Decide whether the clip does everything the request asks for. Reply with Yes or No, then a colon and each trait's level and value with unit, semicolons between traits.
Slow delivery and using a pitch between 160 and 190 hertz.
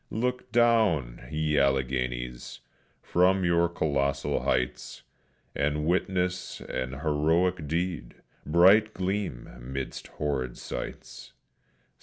No: slow, 90 wpm; very low, 75 Hz